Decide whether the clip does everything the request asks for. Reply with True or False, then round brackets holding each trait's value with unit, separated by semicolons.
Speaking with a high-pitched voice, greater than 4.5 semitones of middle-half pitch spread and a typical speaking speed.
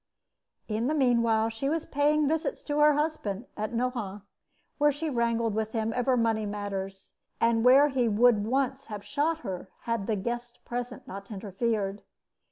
False (235 Hz; 4.2 semitones; 165 wpm)